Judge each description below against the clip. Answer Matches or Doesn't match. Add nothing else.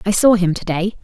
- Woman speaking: Matches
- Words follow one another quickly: Matches